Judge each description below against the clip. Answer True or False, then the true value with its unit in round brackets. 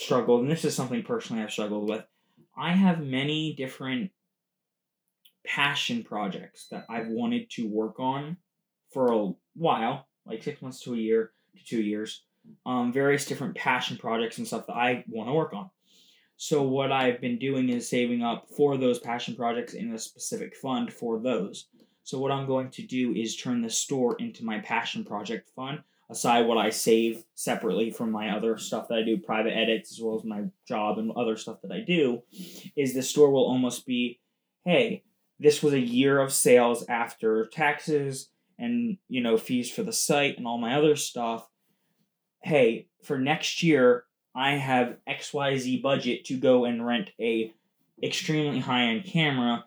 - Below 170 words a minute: False (180 wpm)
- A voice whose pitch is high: False (135 Hz)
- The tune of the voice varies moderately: False (7.1 semitones)